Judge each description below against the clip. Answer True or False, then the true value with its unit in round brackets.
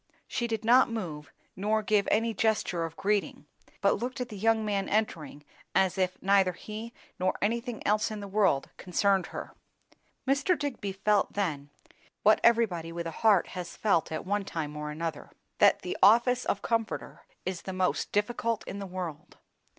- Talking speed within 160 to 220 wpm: True (175 wpm)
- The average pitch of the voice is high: True (200 Hz)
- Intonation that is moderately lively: True (3.8 semitones)